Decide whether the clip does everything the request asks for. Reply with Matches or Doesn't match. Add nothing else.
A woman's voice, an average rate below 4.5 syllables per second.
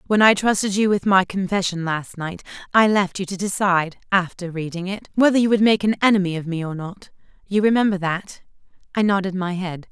Doesn't match